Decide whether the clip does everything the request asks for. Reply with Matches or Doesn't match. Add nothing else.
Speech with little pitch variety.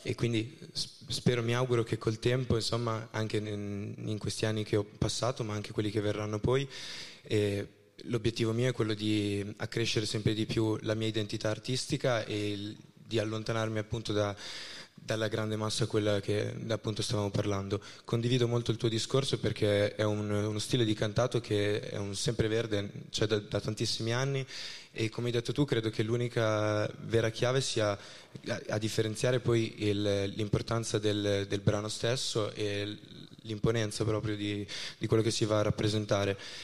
Matches